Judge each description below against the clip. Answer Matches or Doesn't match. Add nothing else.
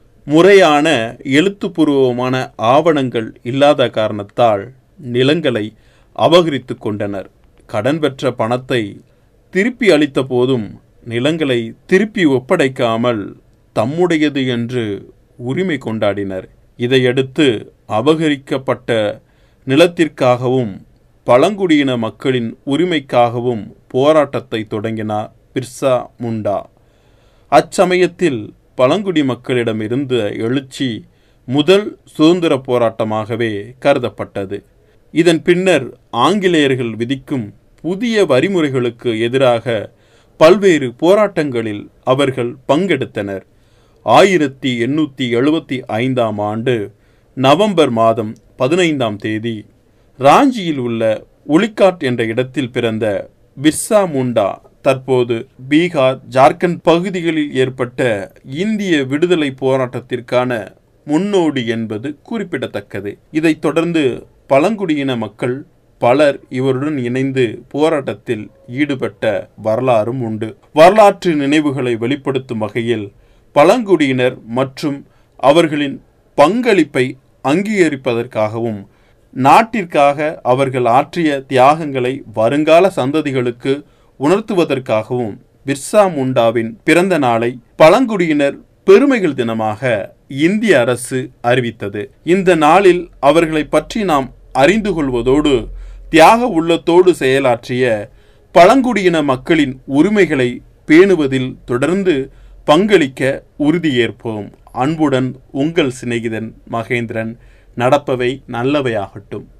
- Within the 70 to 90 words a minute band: Matches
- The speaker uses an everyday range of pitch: Matches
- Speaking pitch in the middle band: Doesn't match